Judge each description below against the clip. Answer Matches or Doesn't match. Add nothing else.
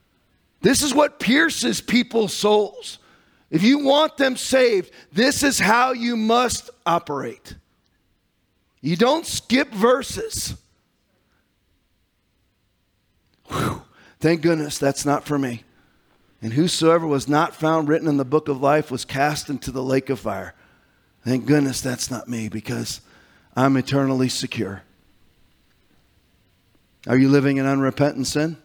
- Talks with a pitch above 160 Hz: Doesn't match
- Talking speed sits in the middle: Doesn't match